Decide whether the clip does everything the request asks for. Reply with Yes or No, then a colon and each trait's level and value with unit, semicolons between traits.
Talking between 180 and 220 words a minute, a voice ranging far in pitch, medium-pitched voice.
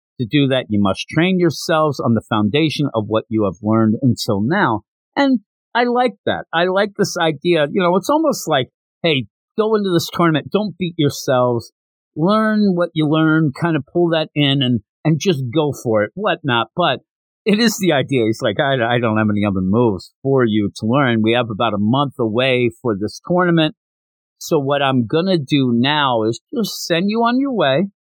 Yes: average, 200 wpm; wide, 7.0 semitones; medium, 145 Hz